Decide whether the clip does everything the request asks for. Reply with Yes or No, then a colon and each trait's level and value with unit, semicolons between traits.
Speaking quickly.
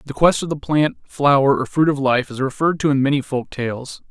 Yes: fast, 250 wpm